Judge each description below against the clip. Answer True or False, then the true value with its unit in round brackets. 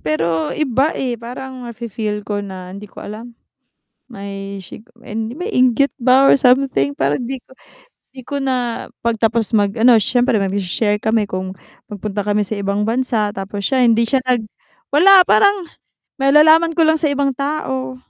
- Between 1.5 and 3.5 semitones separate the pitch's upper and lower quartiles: False (4.6 semitones)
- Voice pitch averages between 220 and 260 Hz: True (235 Hz)